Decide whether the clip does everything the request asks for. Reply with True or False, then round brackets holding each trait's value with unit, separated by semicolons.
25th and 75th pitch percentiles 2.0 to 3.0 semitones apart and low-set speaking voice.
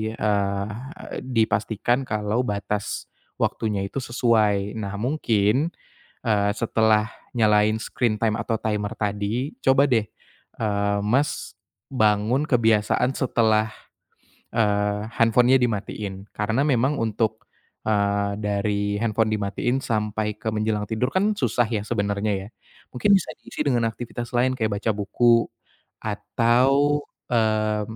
True (2.6 semitones; 110 Hz)